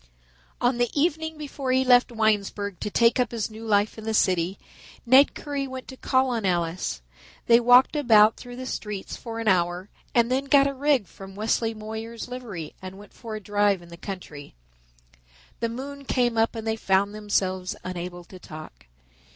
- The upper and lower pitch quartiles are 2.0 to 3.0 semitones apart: No, average, 4.5 semitones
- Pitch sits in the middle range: No, high, 220 Hz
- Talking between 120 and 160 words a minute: No, average, 185 wpm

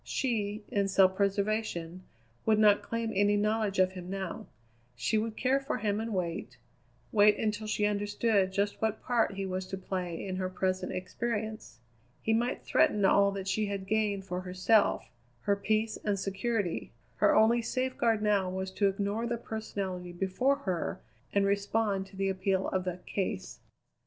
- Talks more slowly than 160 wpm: No, average, 165 wpm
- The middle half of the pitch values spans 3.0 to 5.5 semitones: No, narrow, 2.5 semitones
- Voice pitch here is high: Yes, high, 200 Hz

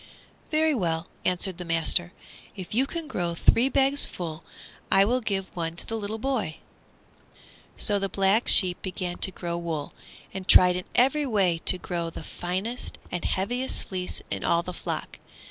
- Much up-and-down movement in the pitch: No, average, 4.7 semitones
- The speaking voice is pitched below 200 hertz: Yes, medium, 185 Hz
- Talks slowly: No, average, 170 wpm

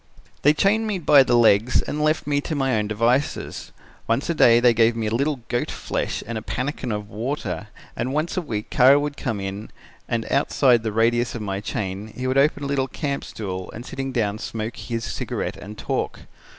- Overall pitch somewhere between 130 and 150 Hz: No, low, 120 Hz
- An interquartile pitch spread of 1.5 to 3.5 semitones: No, average, 4.4 semitones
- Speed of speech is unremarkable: No, fast, 210 wpm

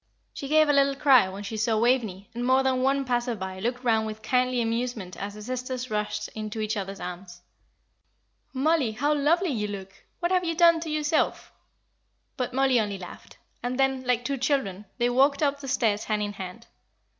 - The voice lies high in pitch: Yes, high, 245 Hz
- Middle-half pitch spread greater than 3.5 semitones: Yes, average, 4.4 semitones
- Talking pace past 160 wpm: Yes, average, 200 wpm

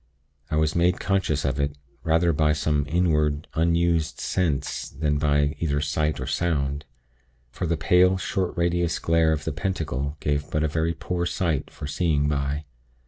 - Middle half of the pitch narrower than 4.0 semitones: Yes, narrow, 2.6 semitones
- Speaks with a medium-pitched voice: No, very low, 80 Hz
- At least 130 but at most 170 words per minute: Yes, average, 165 wpm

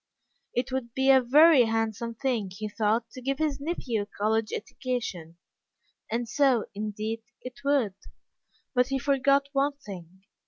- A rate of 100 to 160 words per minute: Yes, average, 150 wpm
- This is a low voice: No, high, 240 Hz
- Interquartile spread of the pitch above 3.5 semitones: Yes, average, 4.1 semitones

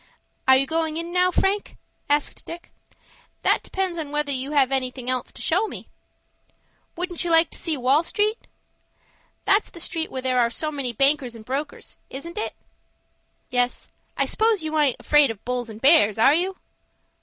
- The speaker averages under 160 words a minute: No, average, 175 wpm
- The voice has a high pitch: Yes, very high, 295 Hz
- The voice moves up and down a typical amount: Yes, average, 4.9 semitones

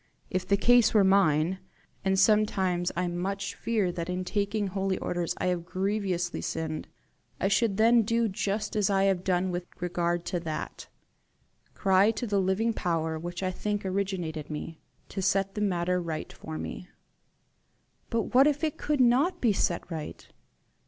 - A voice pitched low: No, high, 190 Hz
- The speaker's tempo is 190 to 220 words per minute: No, average, 165 wpm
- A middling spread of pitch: Yes, average, 3.0 semitones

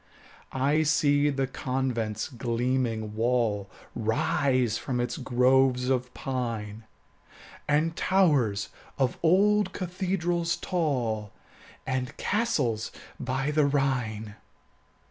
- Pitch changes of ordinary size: Yes, average, 4.4 semitones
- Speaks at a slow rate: Yes, slow, 90 wpm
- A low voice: Yes, low, 130 Hz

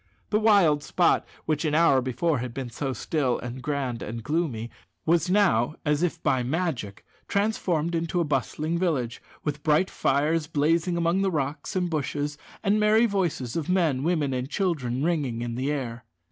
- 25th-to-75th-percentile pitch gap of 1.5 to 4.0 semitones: No, average, 4.7 semitones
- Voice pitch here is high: No, medium, 150 Hz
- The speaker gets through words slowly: No, average, 175 wpm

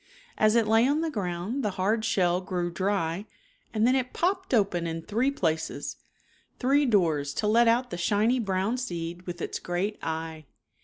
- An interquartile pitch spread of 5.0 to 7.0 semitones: Yes, average, 5.3 semitones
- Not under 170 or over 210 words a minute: Yes, average, 175 wpm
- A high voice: Yes, high, 205 Hz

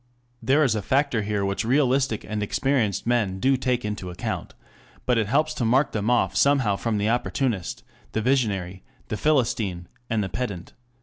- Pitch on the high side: No, low, 115 Hz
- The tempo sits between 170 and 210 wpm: Yes, average, 180 wpm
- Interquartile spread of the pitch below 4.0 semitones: No, average, 4.5 semitones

